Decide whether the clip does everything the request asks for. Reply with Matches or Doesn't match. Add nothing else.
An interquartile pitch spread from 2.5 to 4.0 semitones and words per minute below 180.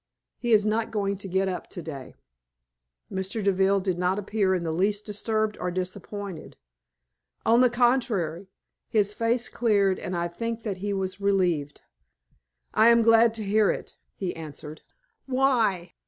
Matches